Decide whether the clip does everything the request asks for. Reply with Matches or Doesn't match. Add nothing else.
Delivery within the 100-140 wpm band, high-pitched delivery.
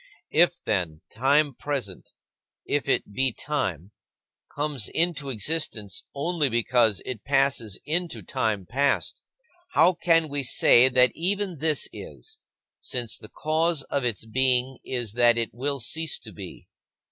Doesn't match